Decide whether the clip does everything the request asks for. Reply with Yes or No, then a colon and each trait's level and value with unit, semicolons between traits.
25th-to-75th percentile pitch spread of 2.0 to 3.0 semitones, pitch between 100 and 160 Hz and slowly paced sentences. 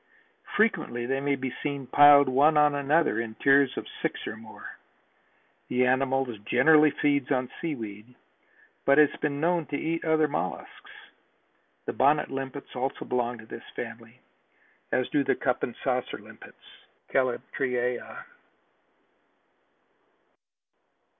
Yes: average, 2.7 semitones; low, 135 Hz; slow, 125 wpm